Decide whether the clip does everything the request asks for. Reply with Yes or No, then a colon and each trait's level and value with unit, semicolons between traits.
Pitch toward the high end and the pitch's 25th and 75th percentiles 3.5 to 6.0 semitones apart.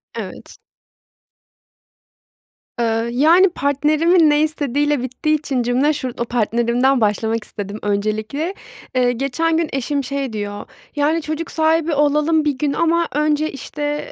Yes: very high, 285 Hz; average, 4.3 semitones